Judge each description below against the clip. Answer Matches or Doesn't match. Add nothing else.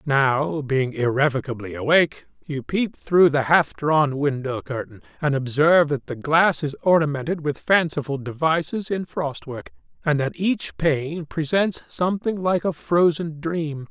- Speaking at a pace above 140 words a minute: Matches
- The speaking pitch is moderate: Matches